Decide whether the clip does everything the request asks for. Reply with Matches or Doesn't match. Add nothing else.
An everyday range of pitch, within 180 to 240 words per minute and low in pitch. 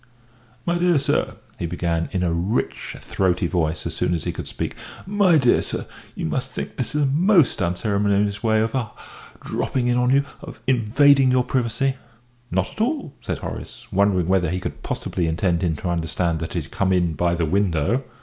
Doesn't match